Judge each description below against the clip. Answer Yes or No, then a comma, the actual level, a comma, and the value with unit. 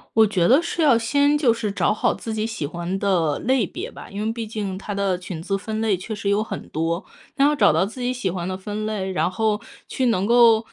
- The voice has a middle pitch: No, high, 215 Hz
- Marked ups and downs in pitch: No, average, 3.4 semitones